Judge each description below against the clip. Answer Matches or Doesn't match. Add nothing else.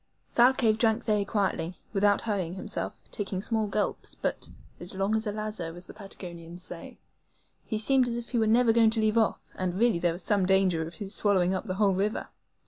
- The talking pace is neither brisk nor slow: Doesn't match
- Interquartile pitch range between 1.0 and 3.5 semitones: Matches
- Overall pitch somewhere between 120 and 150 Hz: Doesn't match